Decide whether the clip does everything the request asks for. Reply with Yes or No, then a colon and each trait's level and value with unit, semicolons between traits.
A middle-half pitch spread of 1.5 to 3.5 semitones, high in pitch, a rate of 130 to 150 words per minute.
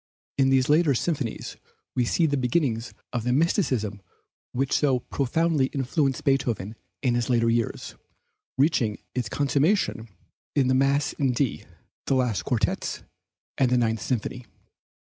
No: average, 3.1 semitones; low, 130 Hz; average, 140 wpm